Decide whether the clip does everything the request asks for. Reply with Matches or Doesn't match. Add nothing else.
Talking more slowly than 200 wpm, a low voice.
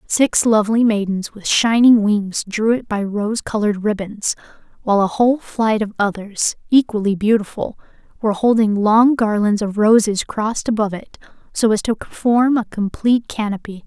Doesn't match